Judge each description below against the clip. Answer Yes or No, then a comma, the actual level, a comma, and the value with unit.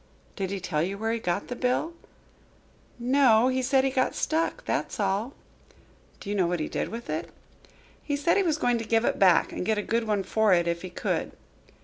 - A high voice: Yes, high, 225 Hz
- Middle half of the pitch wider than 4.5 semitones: Yes, average, 5.1 semitones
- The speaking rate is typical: No, fast, 225 wpm